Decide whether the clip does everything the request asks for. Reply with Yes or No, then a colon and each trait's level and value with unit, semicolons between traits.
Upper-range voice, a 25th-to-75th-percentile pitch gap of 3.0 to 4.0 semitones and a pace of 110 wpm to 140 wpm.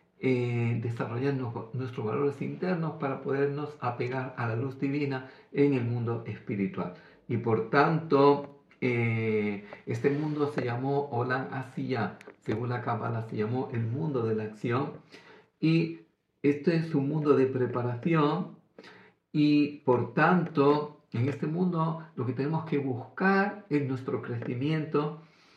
No: medium, 140 Hz; average, 3.4 semitones; average, 135 wpm